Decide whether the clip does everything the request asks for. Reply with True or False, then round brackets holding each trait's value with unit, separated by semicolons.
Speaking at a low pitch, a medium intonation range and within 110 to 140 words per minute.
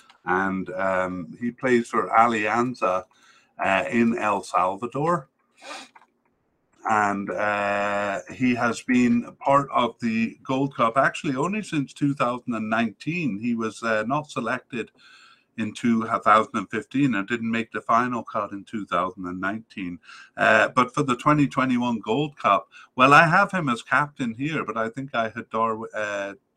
True (120 Hz; 4.8 semitones; 135 wpm)